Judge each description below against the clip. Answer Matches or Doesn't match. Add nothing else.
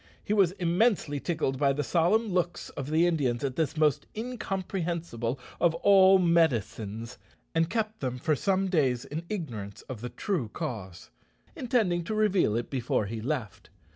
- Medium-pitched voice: Matches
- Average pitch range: Doesn't match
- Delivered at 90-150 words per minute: Doesn't match